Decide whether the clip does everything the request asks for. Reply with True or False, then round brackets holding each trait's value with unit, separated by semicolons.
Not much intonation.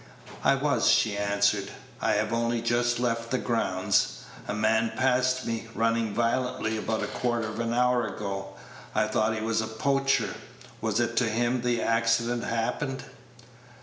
True (1.9 semitones)